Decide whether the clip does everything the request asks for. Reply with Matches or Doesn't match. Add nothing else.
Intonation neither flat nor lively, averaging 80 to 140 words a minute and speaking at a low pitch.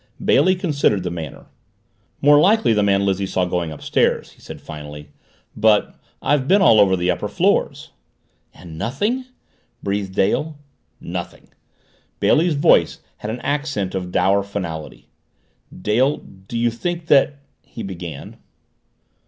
Doesn't match